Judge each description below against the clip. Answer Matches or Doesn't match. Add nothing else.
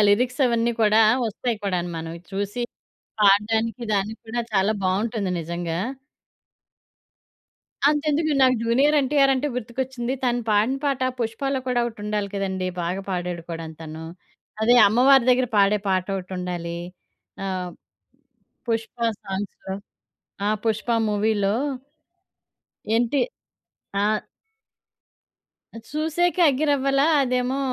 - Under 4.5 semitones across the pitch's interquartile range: Doesn't match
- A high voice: Matches